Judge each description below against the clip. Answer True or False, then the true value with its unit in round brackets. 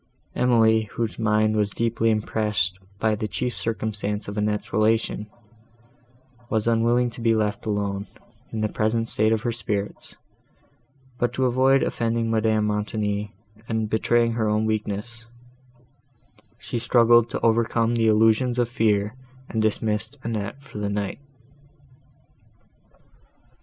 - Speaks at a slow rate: True (130 wpm)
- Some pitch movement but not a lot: False (1.7 semitones)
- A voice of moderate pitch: False (110 Hz)